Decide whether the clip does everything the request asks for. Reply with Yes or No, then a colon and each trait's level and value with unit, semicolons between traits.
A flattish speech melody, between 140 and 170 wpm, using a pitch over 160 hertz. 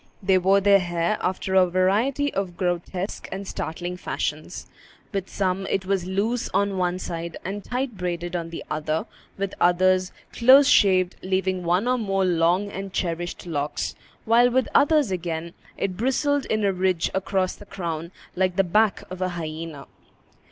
Yes: narrow, 2.3 semitones; average, 165 wpm; medium, 185 Hz